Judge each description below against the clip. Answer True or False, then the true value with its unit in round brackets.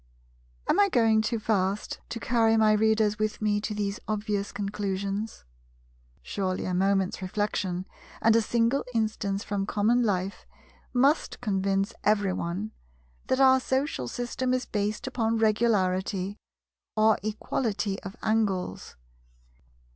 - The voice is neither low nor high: False (210 Hz)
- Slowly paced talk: True (125 wpm)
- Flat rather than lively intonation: True (2.3 semitones)